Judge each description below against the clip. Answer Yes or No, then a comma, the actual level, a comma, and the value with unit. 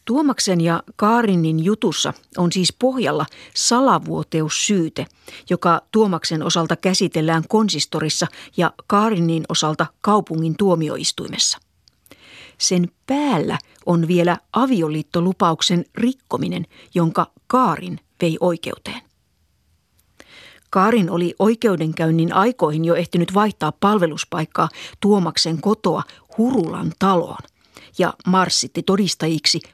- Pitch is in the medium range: Yes, medium, 175 Hz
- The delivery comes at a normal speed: No, slow, 85 wpm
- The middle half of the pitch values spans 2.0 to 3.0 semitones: No, average, 4.2 semitones